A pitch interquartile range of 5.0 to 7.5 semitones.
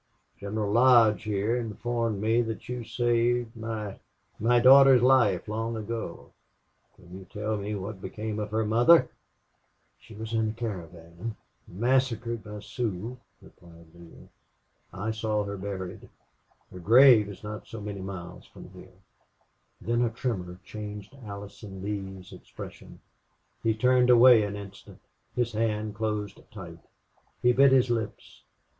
No: average, 2.7 semitones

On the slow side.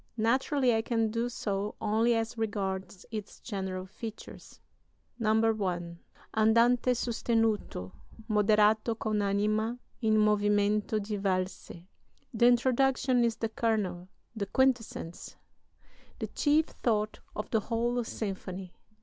Yes: slow, 110 wpm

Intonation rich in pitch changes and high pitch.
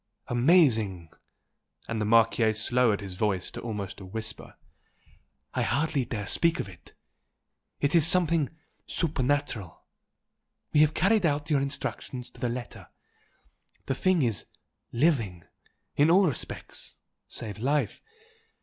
No: wide, 5.8 semitones; low, 125 Hz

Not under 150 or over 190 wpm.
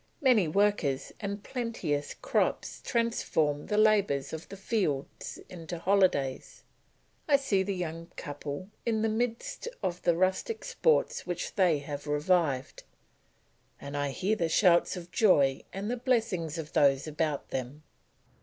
No: average, 140 wpm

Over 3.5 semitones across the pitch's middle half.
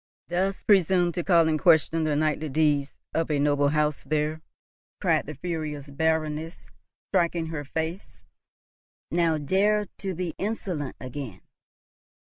No: average, 2.7 semitones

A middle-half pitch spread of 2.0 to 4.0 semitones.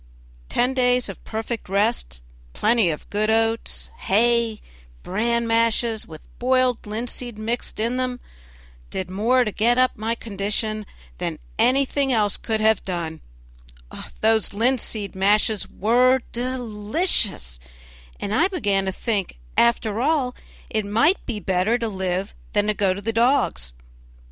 Yes: average, 3.1 semitones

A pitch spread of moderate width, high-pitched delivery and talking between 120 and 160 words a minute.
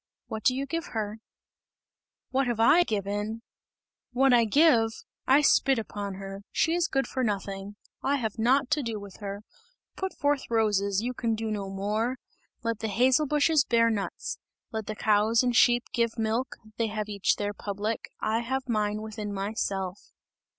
No: average, 3.6 semitones; high, 225 Hz; average, 170 wpm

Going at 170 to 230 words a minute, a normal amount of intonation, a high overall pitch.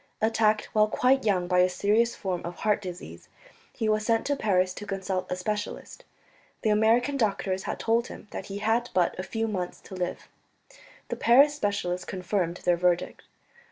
Yes: average, 180 wpm; average, 3.5 semitones; high, 205 Hz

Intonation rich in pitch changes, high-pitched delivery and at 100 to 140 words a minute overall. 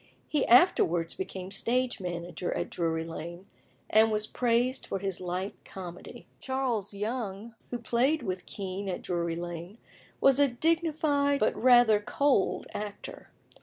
Yes: wide, 5.7 semitones; high, 210 Hz; slow, 135 wpm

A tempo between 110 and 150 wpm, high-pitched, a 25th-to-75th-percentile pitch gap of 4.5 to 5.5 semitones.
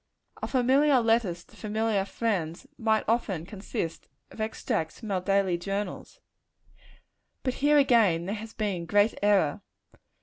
No: slow, 135 wpm; high, 210 Hz; average, 3.7 semitones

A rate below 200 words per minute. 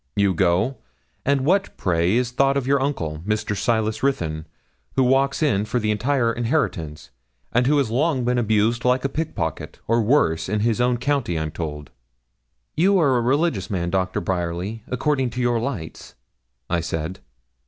Yes: average, 170 wpm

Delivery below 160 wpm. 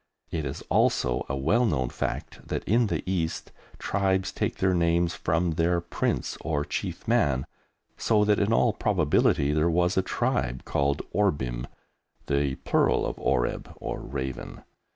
Yes: average, 150 wpm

